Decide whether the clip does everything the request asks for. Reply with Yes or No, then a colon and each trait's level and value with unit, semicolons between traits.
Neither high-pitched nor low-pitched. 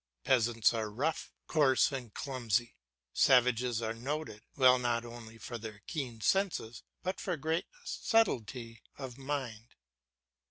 No: low, 120 Hz